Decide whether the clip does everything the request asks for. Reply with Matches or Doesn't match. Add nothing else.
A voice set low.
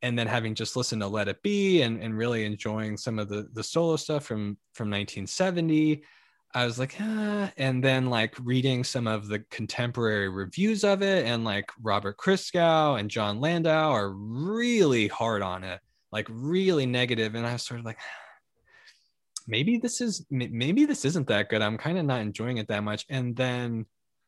Matches